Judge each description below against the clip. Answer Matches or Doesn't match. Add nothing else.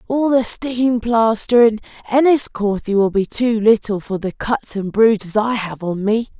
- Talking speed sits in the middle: Matches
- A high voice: Matches